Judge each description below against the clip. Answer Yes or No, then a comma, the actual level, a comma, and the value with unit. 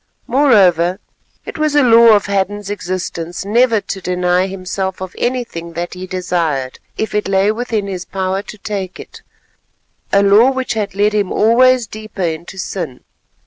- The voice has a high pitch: Yes, high, 195 Hz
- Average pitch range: Yes, average, 3.1 semitones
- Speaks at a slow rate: No, average, 155 wpm